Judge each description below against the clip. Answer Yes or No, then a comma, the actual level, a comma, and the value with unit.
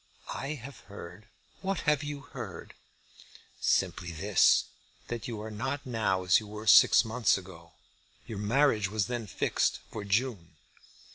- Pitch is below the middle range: Yes, low, 110 Hz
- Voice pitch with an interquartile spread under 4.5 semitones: No, average, 4.9 semitones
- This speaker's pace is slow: No, average, 150 wpm